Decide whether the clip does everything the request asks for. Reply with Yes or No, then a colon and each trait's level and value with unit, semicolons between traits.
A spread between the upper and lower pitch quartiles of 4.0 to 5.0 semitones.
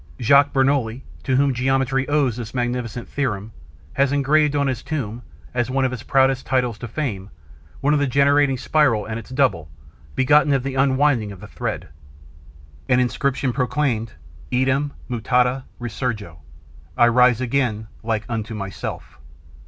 No: average, 3.2 semitones